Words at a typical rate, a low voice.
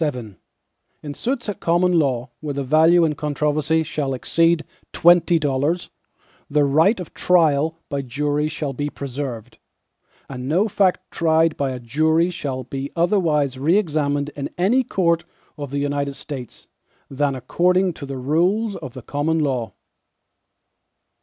No: average, 145 wpm; medium, 150 Hz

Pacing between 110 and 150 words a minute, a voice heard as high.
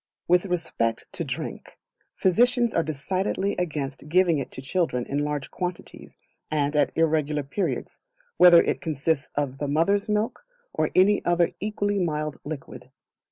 No: average, 145 wpm; medium, 165 Hz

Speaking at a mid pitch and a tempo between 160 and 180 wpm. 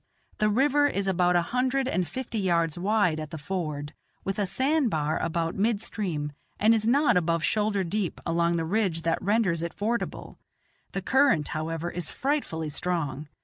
Yes: medium, 180 Hz; average, 175 wpm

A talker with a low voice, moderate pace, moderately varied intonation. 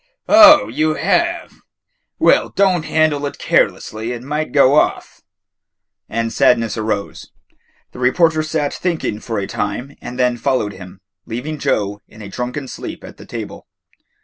No: low, 125 Hz; average, 150 wpm; wide, 5.9 semitones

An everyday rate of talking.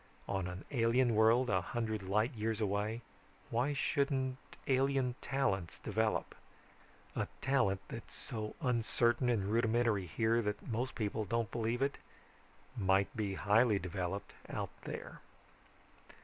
No: slow, 125 wpm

